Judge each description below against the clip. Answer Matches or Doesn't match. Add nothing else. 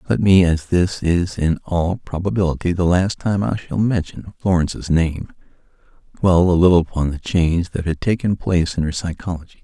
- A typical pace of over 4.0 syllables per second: Matches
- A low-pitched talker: Matches